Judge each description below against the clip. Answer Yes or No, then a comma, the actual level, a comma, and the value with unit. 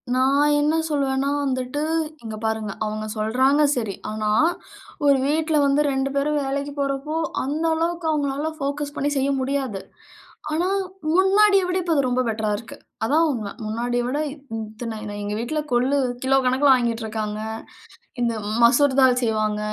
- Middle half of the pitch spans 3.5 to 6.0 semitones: Yes, average, 4.1 semitones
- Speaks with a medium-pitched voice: No, very high, 270 Hz